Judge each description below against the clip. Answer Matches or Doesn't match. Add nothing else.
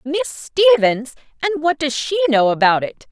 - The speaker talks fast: Doesn't match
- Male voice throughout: Doesn't match